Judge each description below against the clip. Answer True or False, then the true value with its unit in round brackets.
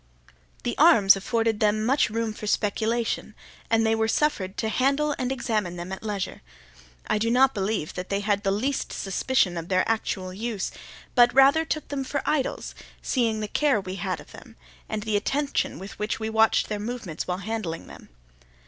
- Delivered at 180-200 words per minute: True (185 wpm)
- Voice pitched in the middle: False (220 Hz)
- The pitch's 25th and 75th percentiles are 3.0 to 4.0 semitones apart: True (3.6 semitones)